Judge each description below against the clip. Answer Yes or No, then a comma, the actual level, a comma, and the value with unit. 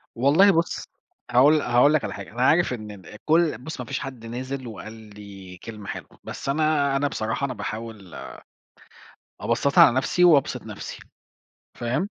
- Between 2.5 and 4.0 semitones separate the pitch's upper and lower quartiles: No, average, 5.3 semitones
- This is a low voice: Yes, low, 125 Hz